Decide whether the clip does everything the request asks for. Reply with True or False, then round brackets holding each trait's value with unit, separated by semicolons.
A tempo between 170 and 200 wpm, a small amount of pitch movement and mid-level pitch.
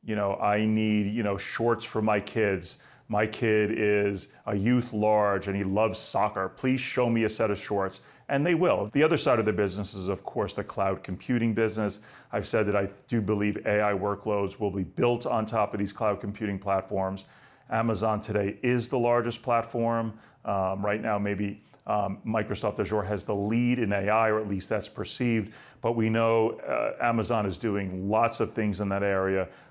False (195 wpm; 2.1 semitones; 105 Hz)